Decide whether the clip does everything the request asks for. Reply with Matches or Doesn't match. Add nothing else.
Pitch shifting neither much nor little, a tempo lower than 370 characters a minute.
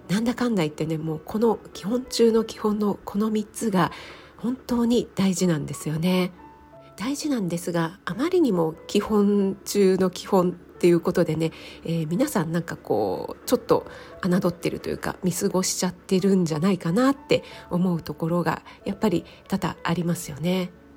Matches